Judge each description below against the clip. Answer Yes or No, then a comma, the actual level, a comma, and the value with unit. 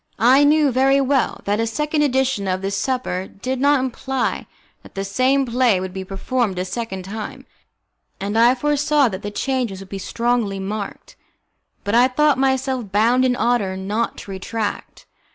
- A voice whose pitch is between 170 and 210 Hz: No, high, 235 Hz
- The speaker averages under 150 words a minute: No, average, 170 wpm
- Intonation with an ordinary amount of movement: Yes, average, 4.9 semitones